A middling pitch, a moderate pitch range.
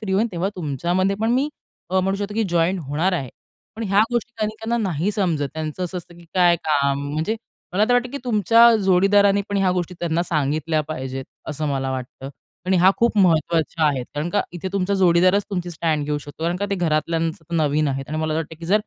Yes: medium, 175 Hz; average, 4.2 semitones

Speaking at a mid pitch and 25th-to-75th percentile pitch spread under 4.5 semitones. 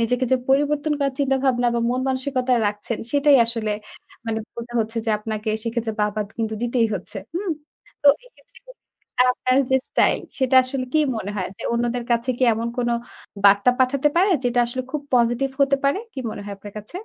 No: high, 245 Hz; average, 3.3 semitones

